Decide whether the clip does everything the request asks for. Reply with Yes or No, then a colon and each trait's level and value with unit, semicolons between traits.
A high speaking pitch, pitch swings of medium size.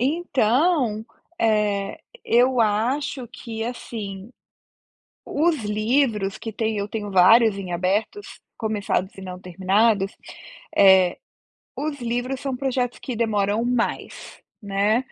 Yes: high, 220 Hz; average, 3.8 semitones